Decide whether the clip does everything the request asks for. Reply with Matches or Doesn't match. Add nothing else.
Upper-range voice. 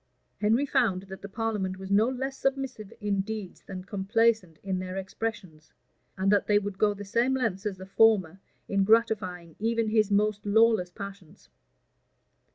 Matches